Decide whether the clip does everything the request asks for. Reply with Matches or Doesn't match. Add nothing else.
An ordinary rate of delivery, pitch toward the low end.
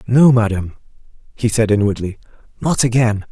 Doesn't match